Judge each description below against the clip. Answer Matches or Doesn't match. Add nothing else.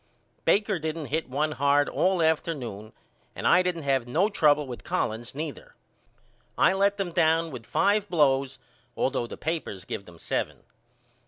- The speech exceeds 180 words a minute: Doesn't match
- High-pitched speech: Doesn't match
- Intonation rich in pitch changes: Doesn't match